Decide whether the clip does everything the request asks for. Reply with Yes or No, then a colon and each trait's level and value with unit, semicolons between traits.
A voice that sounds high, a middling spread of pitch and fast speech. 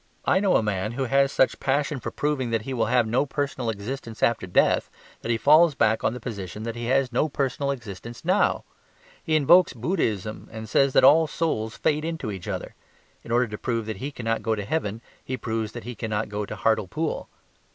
No: low, 120 Hz; average, 4.1 semitones; fast, 215 wpm